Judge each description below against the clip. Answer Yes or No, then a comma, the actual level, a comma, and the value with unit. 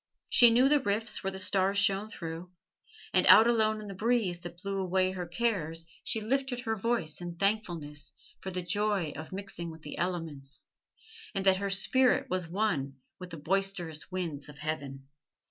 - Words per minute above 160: Yes, average, 180 wpm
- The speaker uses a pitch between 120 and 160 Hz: No, high, 190 Hz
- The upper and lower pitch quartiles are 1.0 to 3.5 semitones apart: No, average, 4.3 semitones